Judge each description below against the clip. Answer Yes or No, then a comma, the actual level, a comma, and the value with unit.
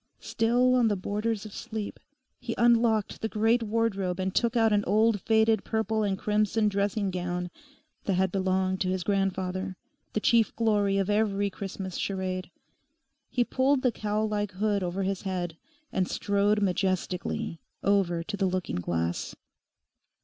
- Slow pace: No, average, 155 wpm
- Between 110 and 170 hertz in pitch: No, high, 200 Hz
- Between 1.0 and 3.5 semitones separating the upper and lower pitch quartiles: Yes, average, 2.8 semitones